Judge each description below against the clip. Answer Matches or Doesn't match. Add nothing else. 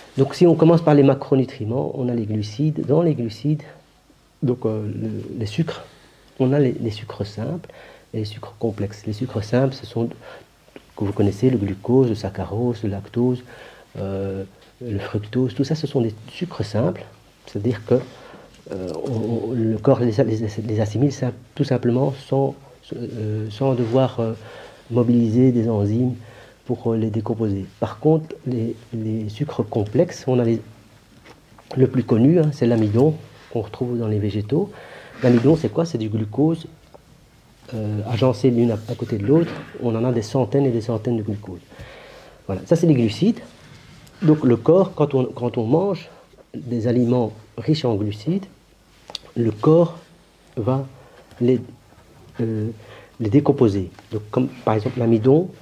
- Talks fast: Doesn't match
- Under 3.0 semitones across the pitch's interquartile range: Doesn't match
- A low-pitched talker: Matches